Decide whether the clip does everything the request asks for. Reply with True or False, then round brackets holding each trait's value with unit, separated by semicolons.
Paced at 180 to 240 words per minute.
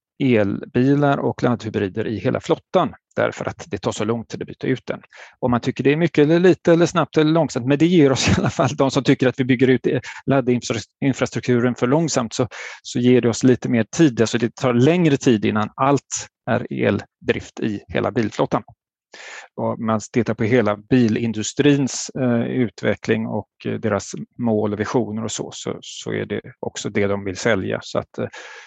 True (195 wpm)